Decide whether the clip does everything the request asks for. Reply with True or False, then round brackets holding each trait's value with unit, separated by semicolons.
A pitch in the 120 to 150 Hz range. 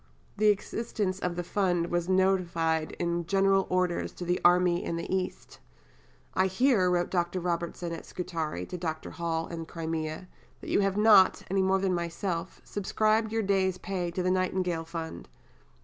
False (180 Hz)